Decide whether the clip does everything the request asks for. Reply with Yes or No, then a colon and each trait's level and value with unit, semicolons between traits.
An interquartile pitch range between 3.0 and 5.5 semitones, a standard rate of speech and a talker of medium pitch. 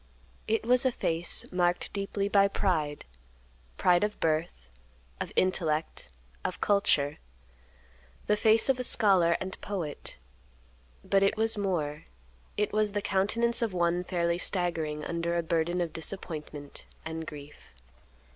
No: average, 4.1 semitones; slow, 130 wpm; medium, 175 Hz